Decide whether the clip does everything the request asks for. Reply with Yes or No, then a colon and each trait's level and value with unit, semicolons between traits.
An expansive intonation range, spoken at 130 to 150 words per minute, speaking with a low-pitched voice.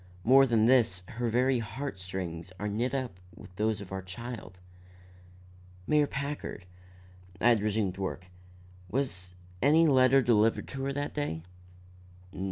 Yes: wide, 5.8 semitones; average, 140 wpm; low, 115 Hz